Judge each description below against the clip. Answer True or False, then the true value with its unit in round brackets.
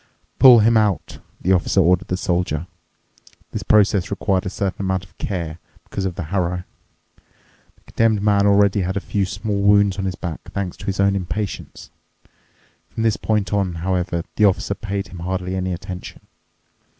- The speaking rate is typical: True (175 wpm)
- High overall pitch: False (95 Hz)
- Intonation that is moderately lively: False (2.0 semitones)